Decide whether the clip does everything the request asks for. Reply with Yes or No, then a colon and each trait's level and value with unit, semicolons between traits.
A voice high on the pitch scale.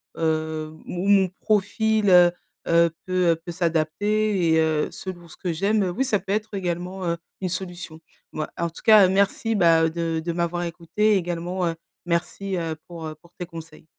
No: medium, 175 Hz